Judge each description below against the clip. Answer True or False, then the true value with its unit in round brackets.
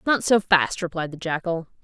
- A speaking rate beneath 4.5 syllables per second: False (5.1 syllables/s)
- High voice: False (175 Hz)